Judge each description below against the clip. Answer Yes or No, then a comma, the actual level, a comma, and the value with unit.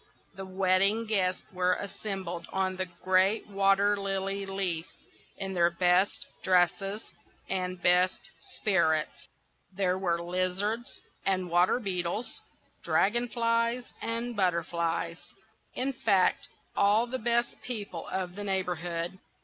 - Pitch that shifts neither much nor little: No, narrow, 2.3 semitones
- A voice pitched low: No, high, 190 Hz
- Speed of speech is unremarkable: No, slow, 110 wpm